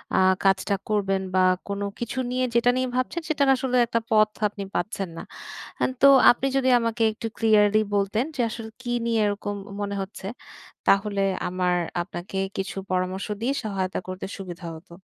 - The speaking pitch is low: No, high, 205 Hz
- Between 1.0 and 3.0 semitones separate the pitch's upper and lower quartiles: No, average, 3.4 semitones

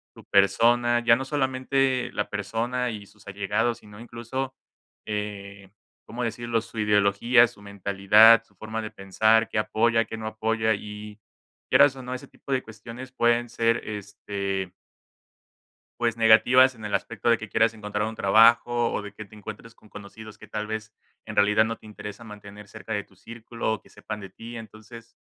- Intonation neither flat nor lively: No, narrow, 2.2 semitones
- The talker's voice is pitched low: Yes, low, 110 Hz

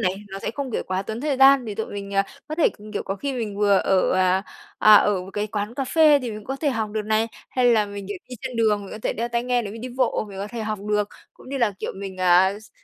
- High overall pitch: Yes, high, 215 Hz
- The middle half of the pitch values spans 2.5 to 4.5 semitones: Yes, average, 3.7 semitones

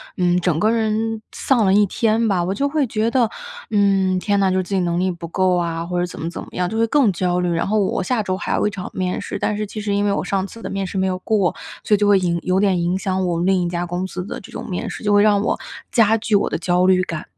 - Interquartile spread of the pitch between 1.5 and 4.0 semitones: Yes, average, 2.8 semitones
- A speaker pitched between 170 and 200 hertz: Yes, high, 190 Hz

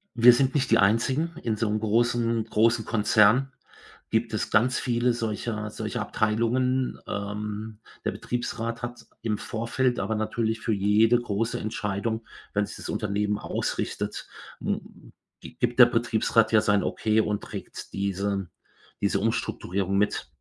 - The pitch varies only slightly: Yes, narrow, 2.3 semitones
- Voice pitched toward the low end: Yes, low, 110 Hz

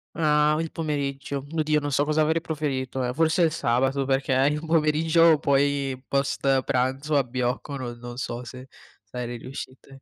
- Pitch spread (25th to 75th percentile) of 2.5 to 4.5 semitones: Yes, average, 2.8 semitones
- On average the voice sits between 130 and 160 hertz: Yes, medium, 140 Hz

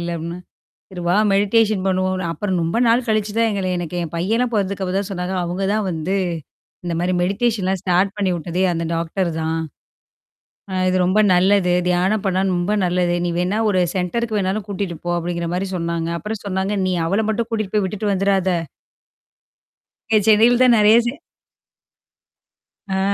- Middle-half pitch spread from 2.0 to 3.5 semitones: Yes, average, 2.8 semitones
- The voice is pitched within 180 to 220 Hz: Yes, high, 190 Hz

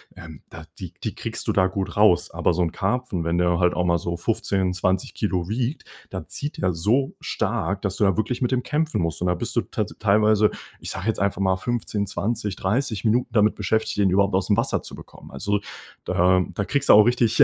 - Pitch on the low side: Yes, low, 100 Hz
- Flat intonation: No, average, 3.5 semitones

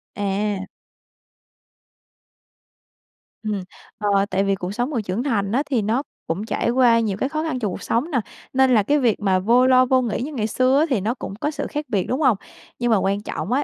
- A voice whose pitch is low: No, high, 230 Hz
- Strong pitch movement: No, average, 4.5 semitones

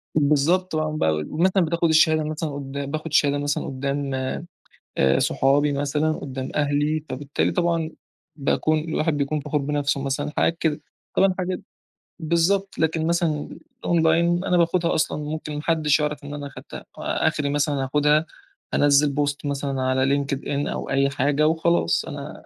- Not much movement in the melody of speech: Yes, narrow, 2.2 semitones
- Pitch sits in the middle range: Yes, medium, 150 Hz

